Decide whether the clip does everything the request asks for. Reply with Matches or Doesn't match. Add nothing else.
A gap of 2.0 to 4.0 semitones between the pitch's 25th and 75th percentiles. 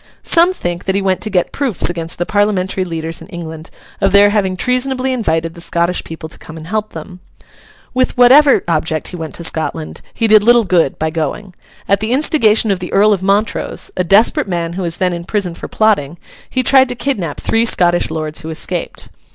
Doesn't match